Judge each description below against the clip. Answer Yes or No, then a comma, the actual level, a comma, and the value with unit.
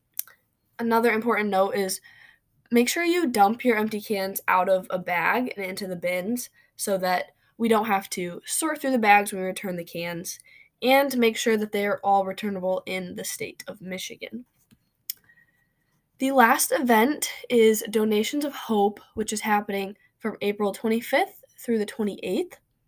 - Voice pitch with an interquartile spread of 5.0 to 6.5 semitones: No, average, 4.0 semitones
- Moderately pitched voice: No, high, 215 Hz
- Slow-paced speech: No, average, 165 wpm